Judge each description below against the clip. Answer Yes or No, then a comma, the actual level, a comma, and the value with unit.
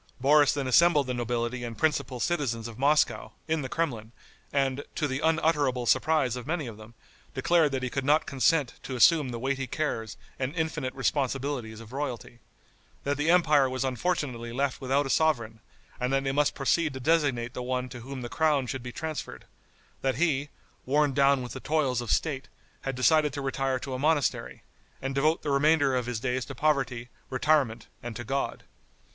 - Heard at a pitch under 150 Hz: Yes, low, 135 Hz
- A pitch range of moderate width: Yes, average, 3.0 semitones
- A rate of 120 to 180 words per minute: No, average, 190 wpm